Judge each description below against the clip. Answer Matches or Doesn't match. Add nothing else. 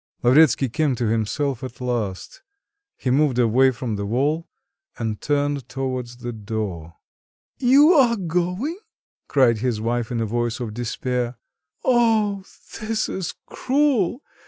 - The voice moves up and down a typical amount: Doesn't match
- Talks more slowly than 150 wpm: Matches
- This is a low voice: Matches